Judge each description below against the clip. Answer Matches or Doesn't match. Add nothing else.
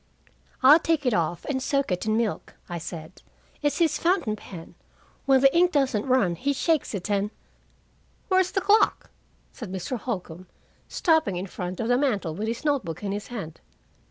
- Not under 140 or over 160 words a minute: Doesn't match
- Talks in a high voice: Matches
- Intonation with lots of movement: Matches